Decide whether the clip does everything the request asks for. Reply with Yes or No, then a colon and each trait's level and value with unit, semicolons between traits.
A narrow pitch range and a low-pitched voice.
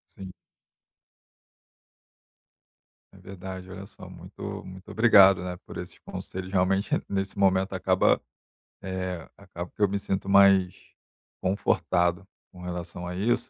Yes: narrow, 1.2 semitones; very low, 95 Hz